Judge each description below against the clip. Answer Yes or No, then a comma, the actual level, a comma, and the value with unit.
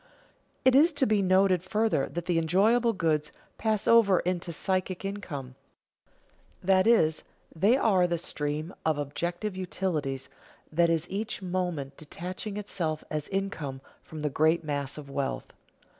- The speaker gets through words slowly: No, average, 145 wpm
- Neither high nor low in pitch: Yes, medium, 175 Hz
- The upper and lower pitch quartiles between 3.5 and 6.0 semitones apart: Yes, average, 4.3 semitones